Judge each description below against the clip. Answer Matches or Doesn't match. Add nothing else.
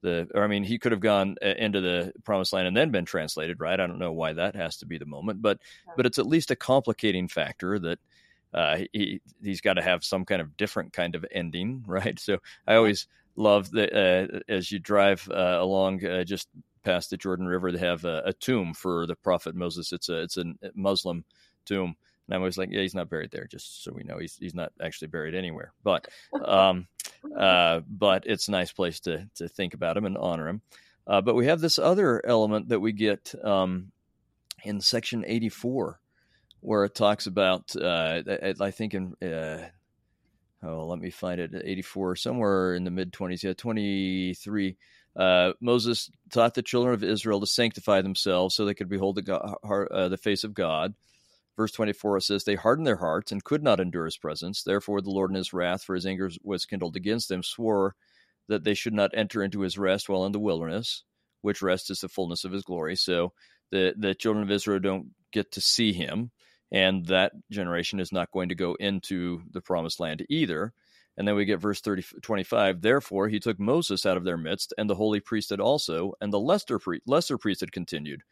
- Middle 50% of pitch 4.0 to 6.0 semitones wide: Doesn't match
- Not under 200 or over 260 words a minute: Matches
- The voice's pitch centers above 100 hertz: Doesn't match